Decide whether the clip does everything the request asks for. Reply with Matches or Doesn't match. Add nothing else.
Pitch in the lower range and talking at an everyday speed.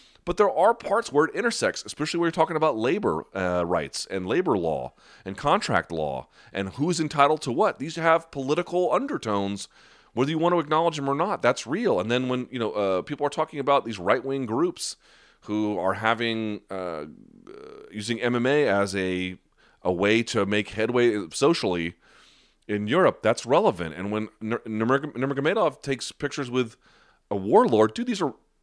Matches